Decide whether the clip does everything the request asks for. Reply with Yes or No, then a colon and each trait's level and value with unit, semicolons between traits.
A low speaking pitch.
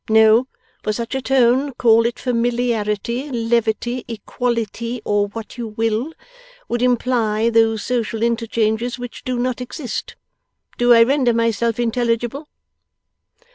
No: high, 235 Hz